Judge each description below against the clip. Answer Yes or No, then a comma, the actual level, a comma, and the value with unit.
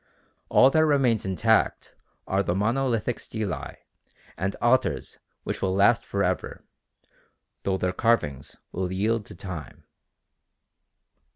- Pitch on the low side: Yes, low, 100 Hz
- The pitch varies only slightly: No, average, 4.0 semitones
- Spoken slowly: Yes, slow, 115 wpm